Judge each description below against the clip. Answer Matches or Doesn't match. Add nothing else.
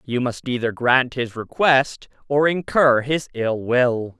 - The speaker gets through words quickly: Doesn't match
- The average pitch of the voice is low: Matches